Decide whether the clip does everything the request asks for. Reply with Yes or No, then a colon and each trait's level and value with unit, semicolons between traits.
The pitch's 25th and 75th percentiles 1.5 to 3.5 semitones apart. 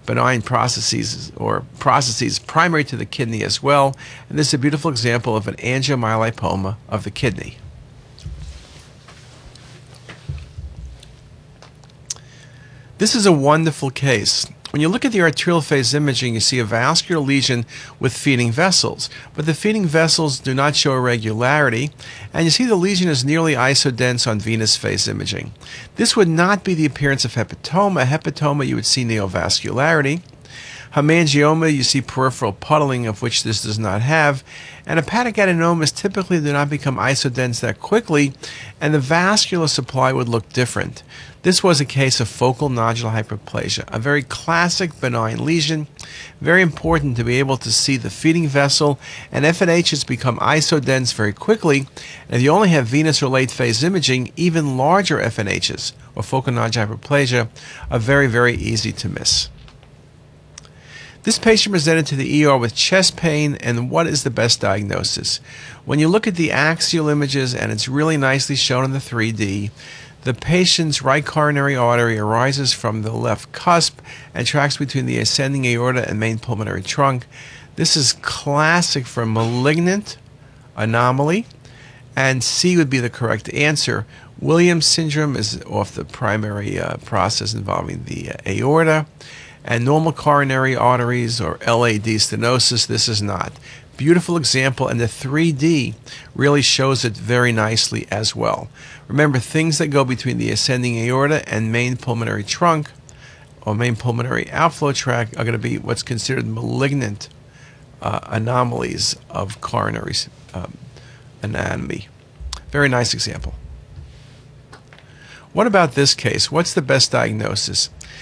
No: average, 4.3 semitones